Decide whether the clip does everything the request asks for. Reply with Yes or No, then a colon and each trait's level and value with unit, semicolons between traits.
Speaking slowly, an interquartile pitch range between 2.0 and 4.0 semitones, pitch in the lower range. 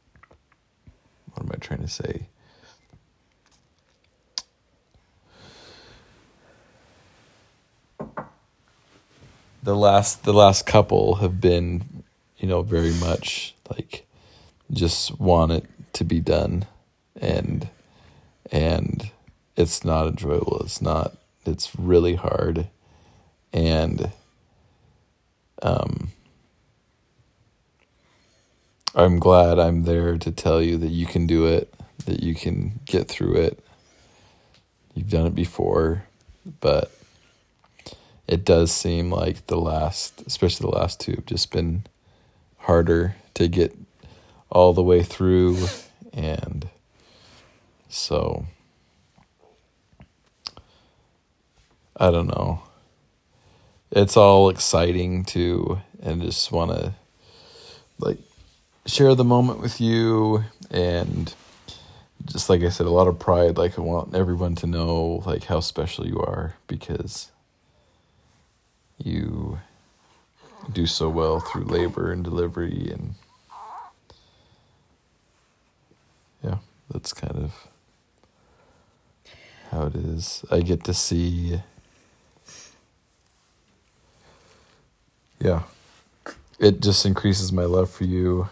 Yes: slow, 100 wpm; narrow, 2.5 semitones; very low, 90 Hz